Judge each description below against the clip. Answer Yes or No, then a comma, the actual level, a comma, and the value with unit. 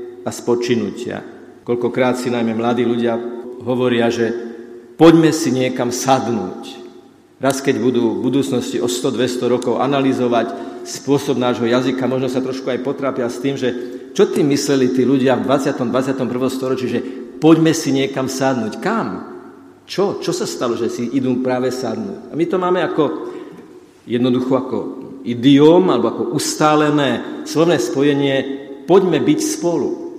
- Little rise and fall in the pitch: Yes, narrow, 2.2 semitones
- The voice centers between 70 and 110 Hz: No, low, 130 Hz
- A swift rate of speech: No, average, 145 wpm